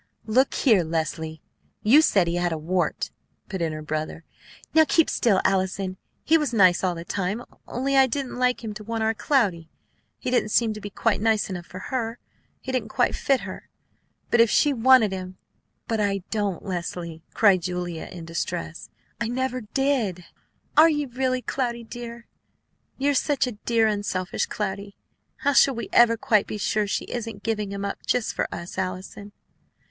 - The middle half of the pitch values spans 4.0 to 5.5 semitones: Yes, average, 5.0 semitones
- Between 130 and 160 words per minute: No, average, 185 wpm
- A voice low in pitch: No, high, 210 Hz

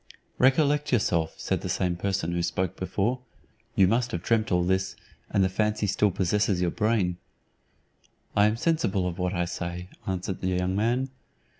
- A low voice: Yes, very low, 95 Hz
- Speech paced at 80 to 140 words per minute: No, average, 170 wpm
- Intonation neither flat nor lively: Yes, average, 3.5 semitones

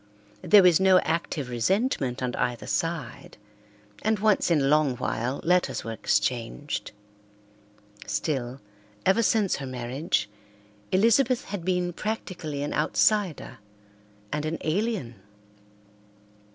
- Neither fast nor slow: No, slow, 110 wpm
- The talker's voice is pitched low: No, medium, 160 Hz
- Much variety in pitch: Yes, wide, 7.0 semitones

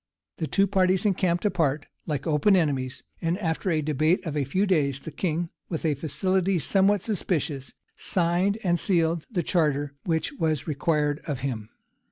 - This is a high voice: No, medium, 165 Hz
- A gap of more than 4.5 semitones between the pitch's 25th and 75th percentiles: No, average, 4.0 semitones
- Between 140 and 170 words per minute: Yes, average, 165 wpm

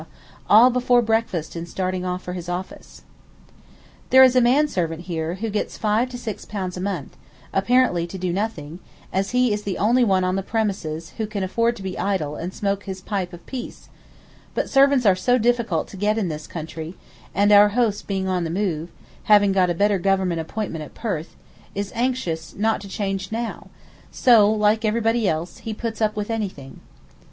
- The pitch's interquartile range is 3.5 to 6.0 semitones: Yes, average, 3.8 semitones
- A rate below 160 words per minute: No, average, 190 wpm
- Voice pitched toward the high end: Yes, high, 200 Hz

